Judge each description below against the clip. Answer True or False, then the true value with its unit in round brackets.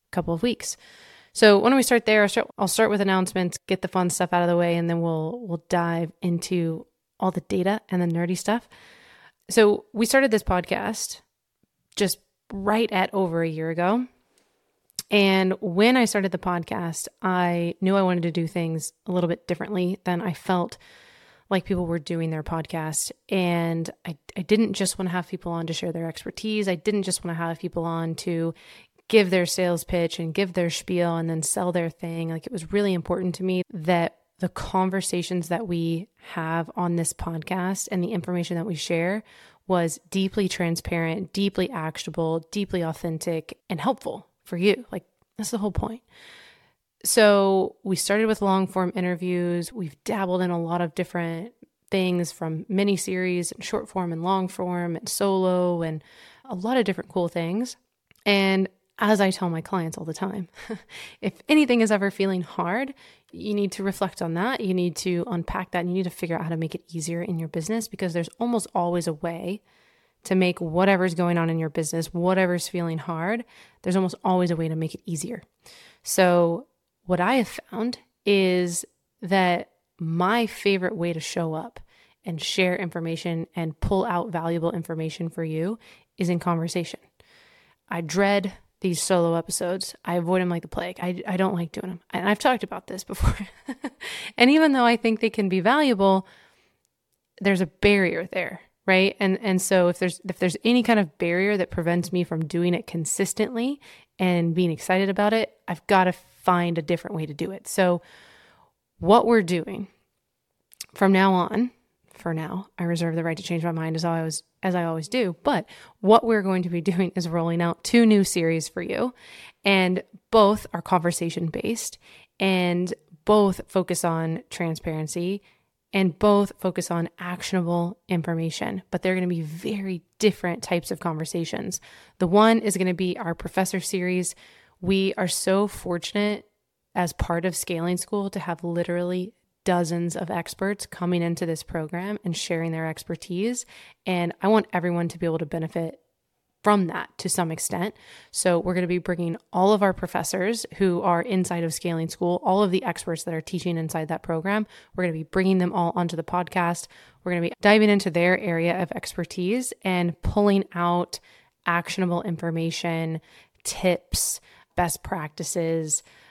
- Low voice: False (180 Hz)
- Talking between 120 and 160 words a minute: False (185 wpm)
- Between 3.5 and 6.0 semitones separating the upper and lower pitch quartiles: False (2.6 semitones)